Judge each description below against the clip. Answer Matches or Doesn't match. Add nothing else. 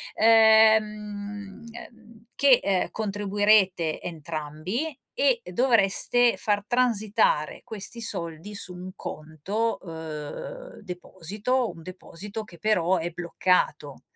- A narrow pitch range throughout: Doesn't match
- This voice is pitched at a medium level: Doesn't match